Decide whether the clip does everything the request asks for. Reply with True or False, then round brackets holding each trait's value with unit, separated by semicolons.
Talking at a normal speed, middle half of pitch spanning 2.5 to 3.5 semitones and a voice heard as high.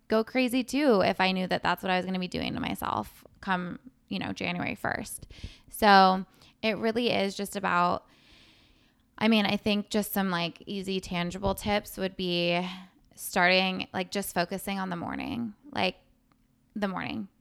True (170 wpm; 2.9 semitones; 195 Hz)